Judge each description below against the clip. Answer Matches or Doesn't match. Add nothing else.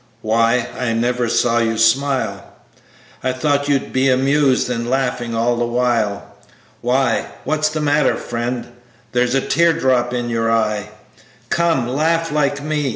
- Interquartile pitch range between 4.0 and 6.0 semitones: Doesn't match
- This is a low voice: Matches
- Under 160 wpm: Matches